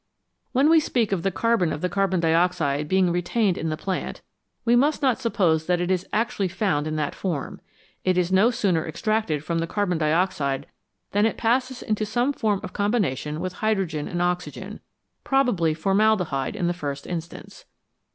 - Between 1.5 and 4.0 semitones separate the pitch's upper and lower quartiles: No, average, 5.0 semitones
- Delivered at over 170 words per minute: Yes, average, 180 wpm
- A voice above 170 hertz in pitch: Yes, medium, 185 Hz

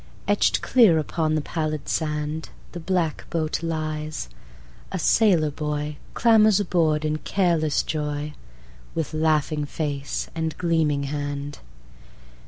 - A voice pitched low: No, medium, 155 Hz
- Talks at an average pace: No, slow, 100 wpm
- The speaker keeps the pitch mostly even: Yes, narrow, 1.8 semitones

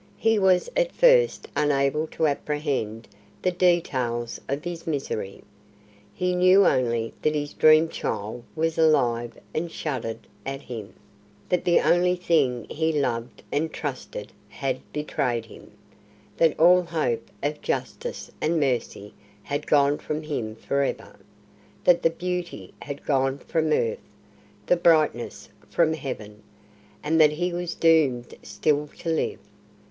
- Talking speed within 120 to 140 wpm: Yes, slow, 135 wpm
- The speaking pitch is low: No, medium, 150 Hz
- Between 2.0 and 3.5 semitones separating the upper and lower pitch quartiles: No, average, 4.8 semitones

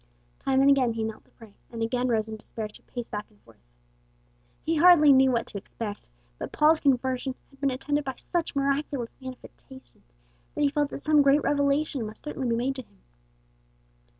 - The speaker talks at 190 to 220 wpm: Yes, average, 195 wpm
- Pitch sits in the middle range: No, very high, 265 Hz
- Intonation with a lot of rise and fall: No, average, 3.7 semitones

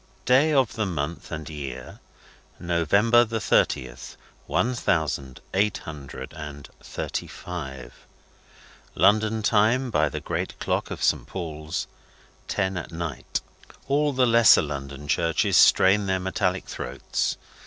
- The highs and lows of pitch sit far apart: Yes, wide, 6.5 semitones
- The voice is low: Yes, very low, 90 Hz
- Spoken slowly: Yes, slow, 125 wpm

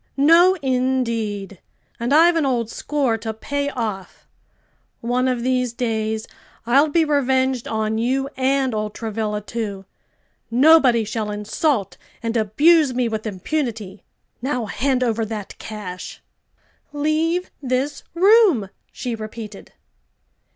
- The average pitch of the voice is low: No, high, 240 Hz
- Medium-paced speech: No, slow, 120 wpm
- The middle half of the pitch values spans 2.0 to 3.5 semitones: No, average, 4.3 semitones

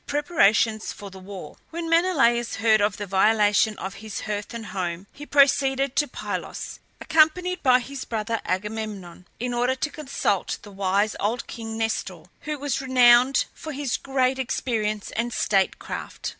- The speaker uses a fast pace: No, average, 155 wpm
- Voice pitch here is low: No, high, 230 Hz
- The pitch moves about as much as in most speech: Yes, average, 4.7 semitones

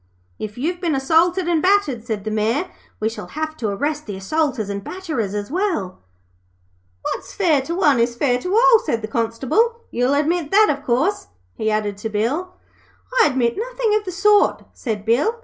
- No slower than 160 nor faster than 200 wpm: Yes, average, 185 wpm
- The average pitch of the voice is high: Yes, very high, 285 Hz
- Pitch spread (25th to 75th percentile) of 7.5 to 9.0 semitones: Yes, wide, 8.3 semitones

